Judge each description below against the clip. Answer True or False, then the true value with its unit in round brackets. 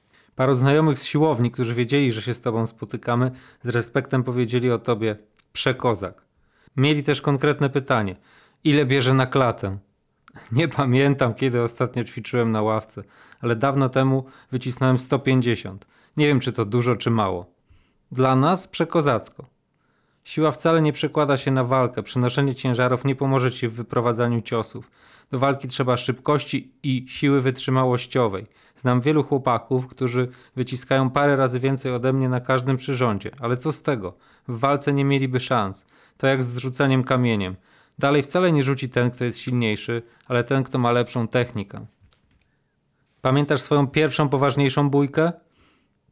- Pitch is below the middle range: True (130 Hz)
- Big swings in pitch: False (2.5 semitones)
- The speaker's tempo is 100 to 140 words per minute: False (150 wpm)